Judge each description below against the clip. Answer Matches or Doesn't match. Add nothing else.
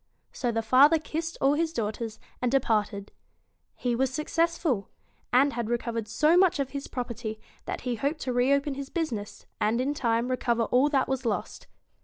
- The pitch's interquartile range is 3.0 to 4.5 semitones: Matches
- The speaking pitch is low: Doesn't match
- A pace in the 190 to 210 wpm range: Doesn't match